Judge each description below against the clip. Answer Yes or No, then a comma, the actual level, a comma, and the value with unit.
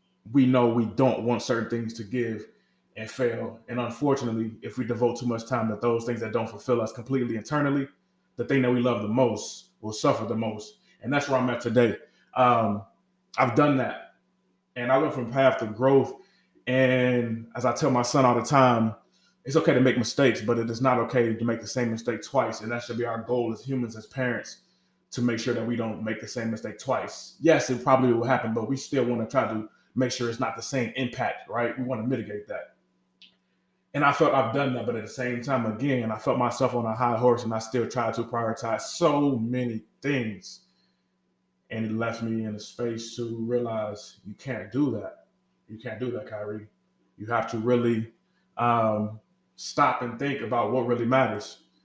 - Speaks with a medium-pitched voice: No, low, 120 Hz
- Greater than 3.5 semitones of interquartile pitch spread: No, narrow, 2.4 semitones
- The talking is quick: Yes, fast, 215 wpm